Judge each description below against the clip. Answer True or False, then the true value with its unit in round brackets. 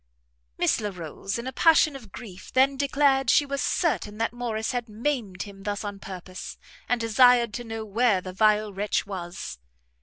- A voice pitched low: False (220 Hz)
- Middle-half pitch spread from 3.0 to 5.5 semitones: True (4.1 semitones)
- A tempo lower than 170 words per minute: False (175 wpm)